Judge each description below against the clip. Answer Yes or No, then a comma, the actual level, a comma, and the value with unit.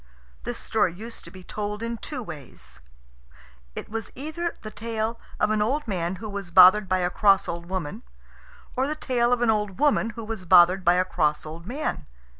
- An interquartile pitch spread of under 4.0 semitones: No, average, 4.4 semitones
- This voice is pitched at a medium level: No, high, 210 Hz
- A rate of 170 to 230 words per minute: Yes, average, 200 wpm